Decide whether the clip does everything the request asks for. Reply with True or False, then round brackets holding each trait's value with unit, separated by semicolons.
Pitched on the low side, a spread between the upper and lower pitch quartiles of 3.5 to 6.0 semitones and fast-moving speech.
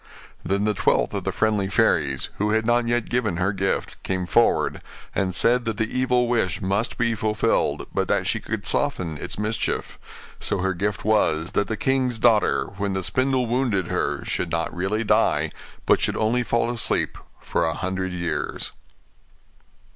False (105 Hz; 3.9 semitones; 175 wpm)